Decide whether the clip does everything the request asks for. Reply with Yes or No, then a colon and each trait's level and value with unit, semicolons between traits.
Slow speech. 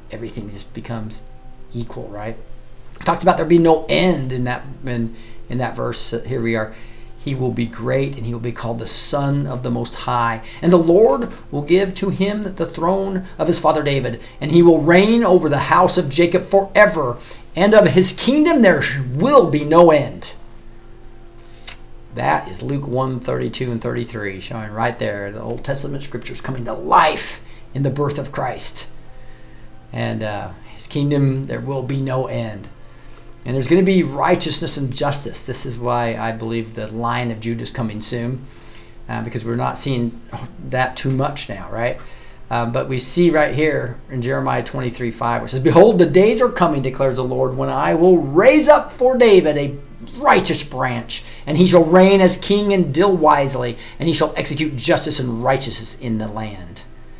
No: average, 185 wpm